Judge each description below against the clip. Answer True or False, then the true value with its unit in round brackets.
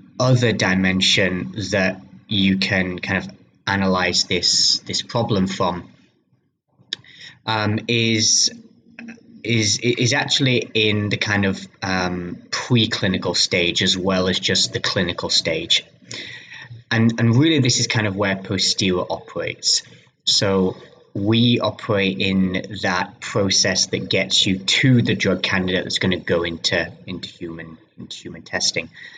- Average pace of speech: False (130 wpm)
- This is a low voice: True (100 Hz)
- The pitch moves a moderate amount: True (3.7 semitones)